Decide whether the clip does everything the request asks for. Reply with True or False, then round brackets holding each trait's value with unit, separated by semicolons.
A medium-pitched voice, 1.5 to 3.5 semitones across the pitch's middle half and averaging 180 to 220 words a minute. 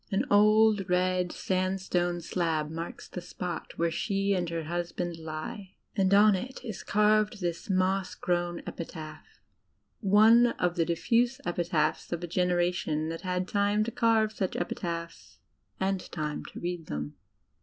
False (180 Hz; 3.1 semitones; 155 wpm)